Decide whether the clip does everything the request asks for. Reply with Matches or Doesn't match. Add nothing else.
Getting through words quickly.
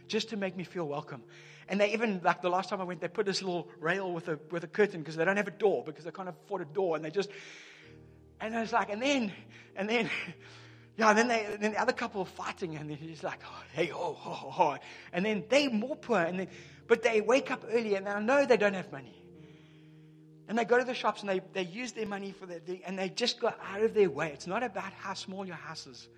Matches